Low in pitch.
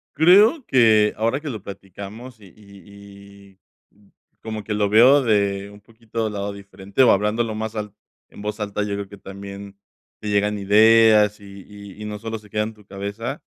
Yes: low, 105 Hz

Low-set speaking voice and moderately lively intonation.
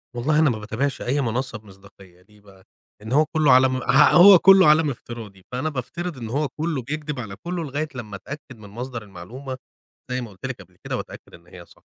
No: low, 125 Hz; wide, 6.1 semitones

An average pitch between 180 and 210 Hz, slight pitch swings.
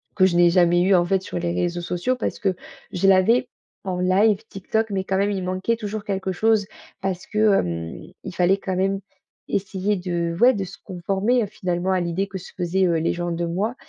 Yes: high, 190 Hz; narrow, 2.2 semitones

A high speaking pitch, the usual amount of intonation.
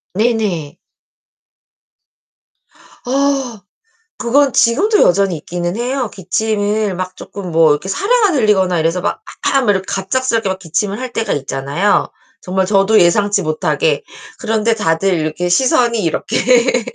Yes: high, 205 Hz; average, 5.0 semitones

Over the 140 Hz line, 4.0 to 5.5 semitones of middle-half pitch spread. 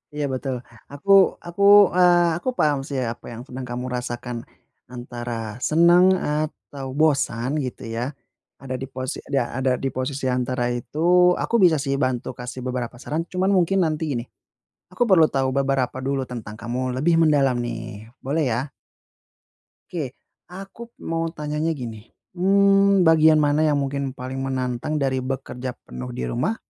No: low, 135 Hz; average, 4.3 semitones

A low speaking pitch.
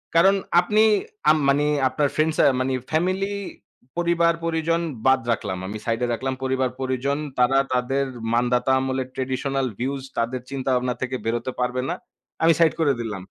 Yes: low, 130 Hz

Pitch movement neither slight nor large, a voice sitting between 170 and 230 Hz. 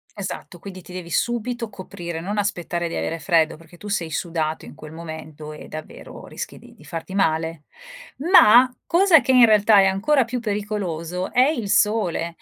Yes: average, 4.7 semitones; medium, 185 Hz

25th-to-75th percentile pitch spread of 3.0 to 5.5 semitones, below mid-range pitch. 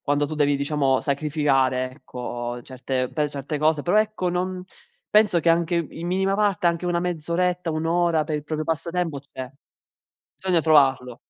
No: average, 3.7 semitones; medium, 155 Hz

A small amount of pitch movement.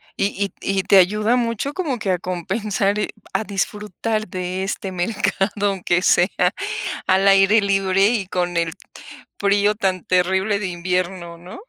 Yes: narrow, 2.3 semitones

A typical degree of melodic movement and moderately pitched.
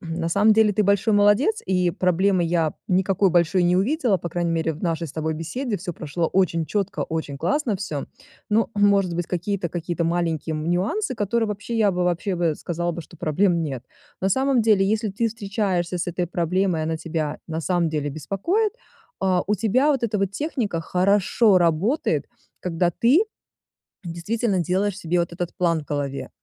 Yes: average, 3.7 semitones; medium, 180 Hz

